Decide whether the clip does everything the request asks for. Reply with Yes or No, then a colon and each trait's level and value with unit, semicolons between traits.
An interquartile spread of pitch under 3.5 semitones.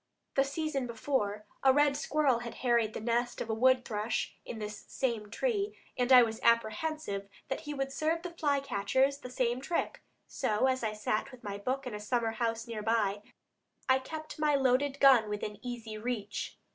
No: average, 3.9 semitones